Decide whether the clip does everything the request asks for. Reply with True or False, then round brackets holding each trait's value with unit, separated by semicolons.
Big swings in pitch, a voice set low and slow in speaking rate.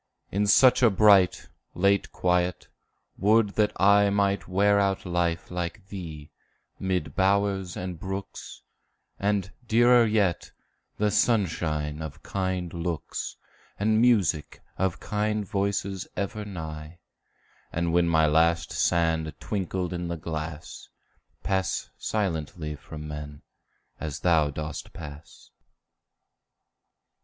False (3.7 semitones; 90 Hz; 110 wpm)